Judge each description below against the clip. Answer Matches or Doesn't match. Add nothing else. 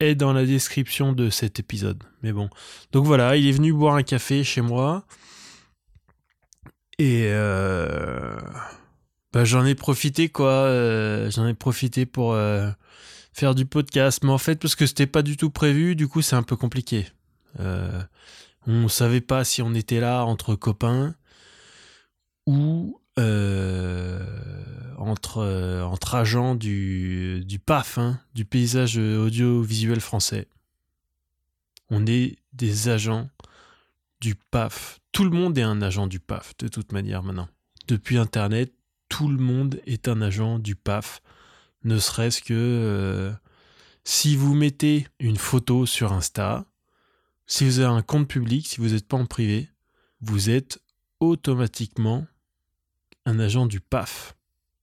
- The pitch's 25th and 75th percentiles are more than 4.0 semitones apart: Matches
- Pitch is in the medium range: Doesn't match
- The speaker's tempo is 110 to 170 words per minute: Matches